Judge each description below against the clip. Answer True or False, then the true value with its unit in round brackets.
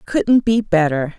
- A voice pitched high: True (195 Hz)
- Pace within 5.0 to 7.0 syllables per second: False (3.8 syllables/s)